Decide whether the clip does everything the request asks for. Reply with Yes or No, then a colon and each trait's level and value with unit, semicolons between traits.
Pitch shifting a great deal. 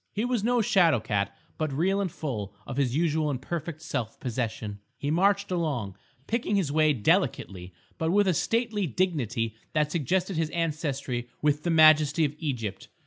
Yes: wide, 5.9 semitones